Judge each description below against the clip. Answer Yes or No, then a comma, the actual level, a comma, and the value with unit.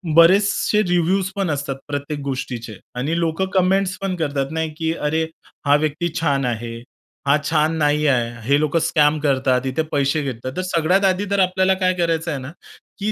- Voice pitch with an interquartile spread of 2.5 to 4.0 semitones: No, average, 4.4 semitones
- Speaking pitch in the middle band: Yes, medium, 155 Hz